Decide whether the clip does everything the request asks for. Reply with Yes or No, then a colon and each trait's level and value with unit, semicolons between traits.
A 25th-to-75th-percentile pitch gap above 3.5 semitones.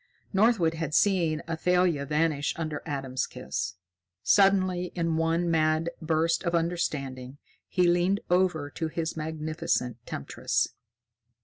No: narrow, 2.6 semitones